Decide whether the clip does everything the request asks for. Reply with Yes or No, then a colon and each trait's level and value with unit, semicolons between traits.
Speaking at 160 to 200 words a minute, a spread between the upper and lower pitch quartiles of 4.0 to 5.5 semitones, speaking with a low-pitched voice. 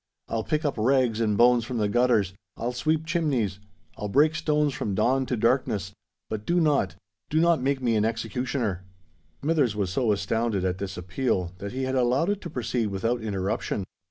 Yes: average, 170 wpm; average, 5.0 semitones; low, 115 Hz